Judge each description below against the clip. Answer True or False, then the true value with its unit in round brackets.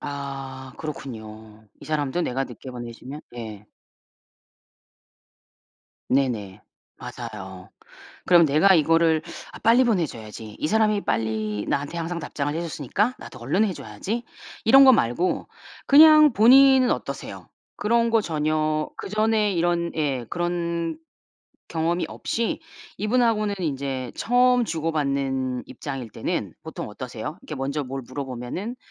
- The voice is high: False (155 Hz)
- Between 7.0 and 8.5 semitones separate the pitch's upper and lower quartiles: True (7.9 semitones)